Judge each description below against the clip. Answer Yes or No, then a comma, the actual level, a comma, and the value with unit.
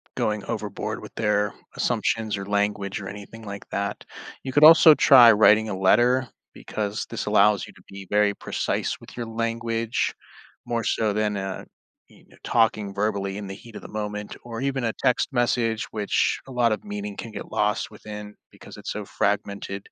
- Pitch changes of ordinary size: No, narrow, 2.3 semitones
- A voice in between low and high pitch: No, low, 105 Hz